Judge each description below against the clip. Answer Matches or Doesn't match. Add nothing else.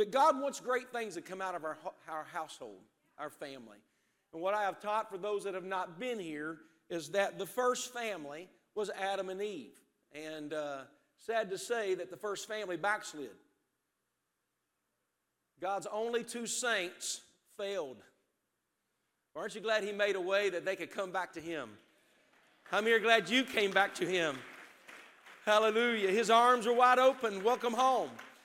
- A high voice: Matches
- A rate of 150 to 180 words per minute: Matches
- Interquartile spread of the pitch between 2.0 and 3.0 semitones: Doesn't match